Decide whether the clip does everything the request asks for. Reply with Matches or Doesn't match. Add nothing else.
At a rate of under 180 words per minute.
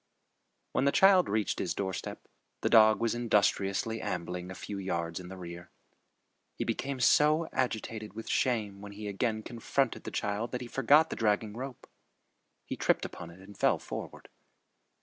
Matches